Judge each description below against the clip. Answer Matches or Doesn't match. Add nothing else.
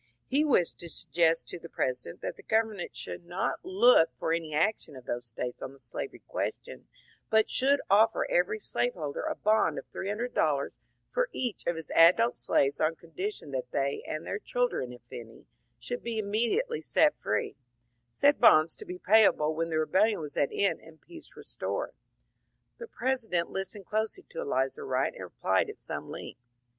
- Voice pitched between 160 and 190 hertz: Matches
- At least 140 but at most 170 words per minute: Doesn't match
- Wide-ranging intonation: Matches